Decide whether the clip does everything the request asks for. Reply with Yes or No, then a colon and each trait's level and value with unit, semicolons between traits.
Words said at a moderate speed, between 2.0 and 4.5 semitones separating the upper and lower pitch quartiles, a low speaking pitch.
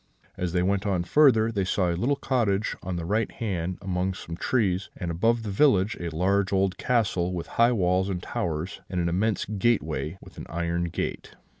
Yes: average, 195 wpm; average, 3.8 semitones; very low, 95 Hz